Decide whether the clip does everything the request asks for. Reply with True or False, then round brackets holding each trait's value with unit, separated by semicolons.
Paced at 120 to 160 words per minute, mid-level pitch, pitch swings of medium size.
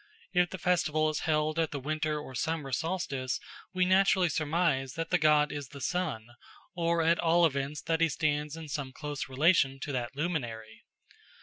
False (180 wpm; 155 Hz; 3.2 semitones)